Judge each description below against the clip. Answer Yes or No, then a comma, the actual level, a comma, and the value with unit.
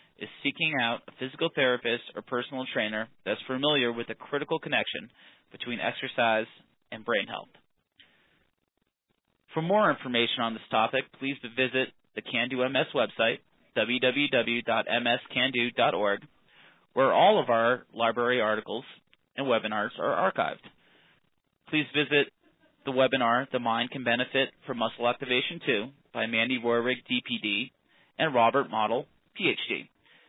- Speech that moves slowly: Yes, slow, 125 wpm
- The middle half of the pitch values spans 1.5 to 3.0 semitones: Yes, narrow, 2.5 semitones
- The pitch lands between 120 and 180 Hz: Yes, low, 125 Hz